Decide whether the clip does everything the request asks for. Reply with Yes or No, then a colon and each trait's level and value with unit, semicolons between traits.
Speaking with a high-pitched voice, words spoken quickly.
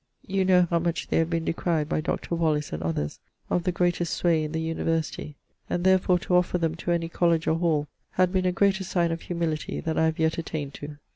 No: medium, 165 Hz; fast, 230 wpm